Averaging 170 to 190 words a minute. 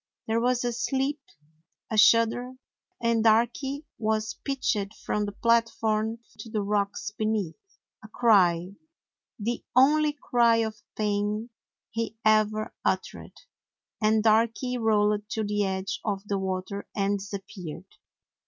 No: slow, 135 wpm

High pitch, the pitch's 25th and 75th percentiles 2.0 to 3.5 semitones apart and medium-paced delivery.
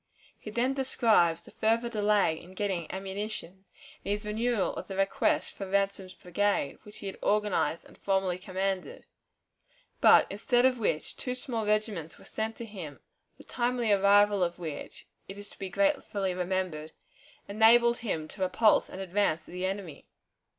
Yes: high, 200 Hz; average, 3.0 semitones; average, 165 wpm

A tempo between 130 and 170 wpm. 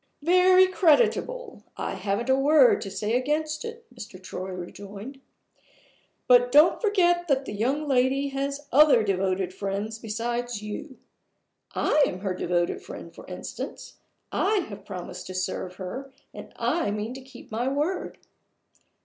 Yes: average, 145 wpm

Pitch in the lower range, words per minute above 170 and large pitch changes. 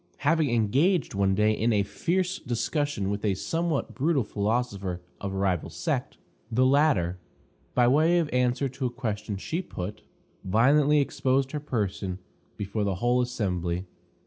No: low, 120 Hz; average, 150 wpm; wide, 6.3 semitones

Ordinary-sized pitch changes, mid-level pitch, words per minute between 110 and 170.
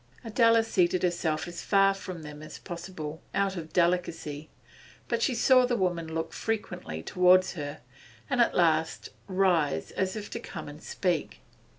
Yes: average, 3.5 semitones; medium, 180 Hz; average, 160 wpm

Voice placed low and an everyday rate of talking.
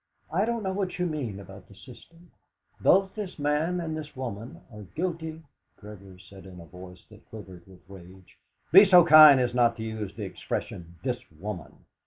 Yes: low, 120 Hz; average, 190 wpm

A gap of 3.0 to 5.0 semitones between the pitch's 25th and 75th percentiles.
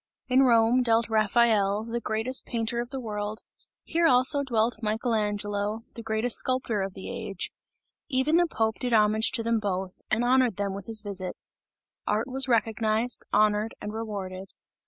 No: narrow, 2.6 semitones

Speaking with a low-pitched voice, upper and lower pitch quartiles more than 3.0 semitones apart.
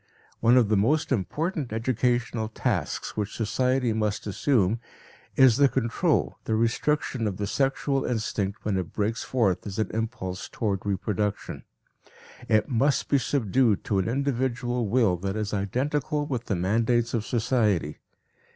Yes: low, 115 Hz; average, 3.8 semitones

